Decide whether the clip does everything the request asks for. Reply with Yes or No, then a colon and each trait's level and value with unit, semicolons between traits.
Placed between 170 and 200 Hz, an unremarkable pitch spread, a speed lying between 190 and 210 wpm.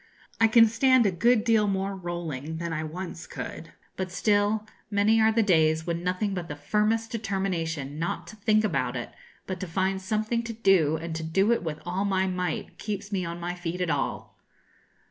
Yes: high, 190 Hz; average, 4.2 semitones; average, 200 wpm